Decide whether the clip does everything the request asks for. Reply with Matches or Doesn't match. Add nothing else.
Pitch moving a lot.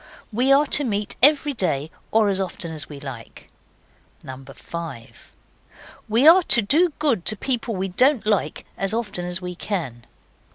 Matches